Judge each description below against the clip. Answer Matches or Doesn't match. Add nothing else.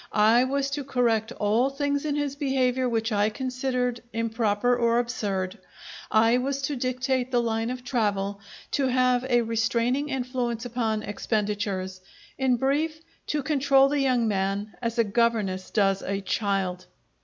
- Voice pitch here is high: Matches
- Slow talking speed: Doesn't match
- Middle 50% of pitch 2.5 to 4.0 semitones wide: Matches